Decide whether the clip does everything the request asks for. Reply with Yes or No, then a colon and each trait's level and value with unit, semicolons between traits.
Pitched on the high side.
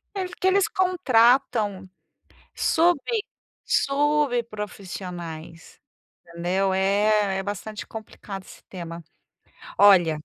Yes: high, 205 Hz